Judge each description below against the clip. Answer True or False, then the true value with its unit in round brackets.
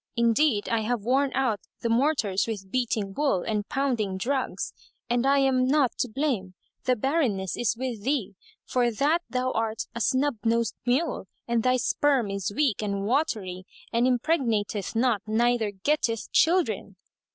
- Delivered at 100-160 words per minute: True (155 wpm)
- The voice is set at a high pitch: True (235 Hz)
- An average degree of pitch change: True (4.1 semitones)